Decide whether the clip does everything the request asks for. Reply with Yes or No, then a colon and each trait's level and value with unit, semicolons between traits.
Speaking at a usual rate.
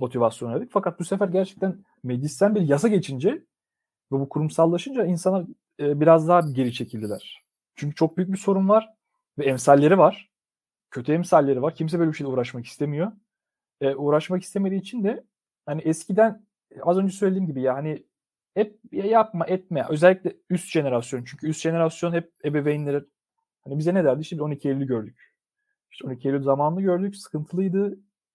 No: fast, 155 wpm